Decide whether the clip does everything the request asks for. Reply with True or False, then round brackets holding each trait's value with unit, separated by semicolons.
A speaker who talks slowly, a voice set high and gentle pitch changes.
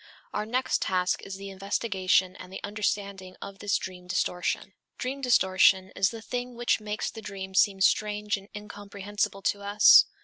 False (165 wpm; 200 Hz; 1.8 semitones)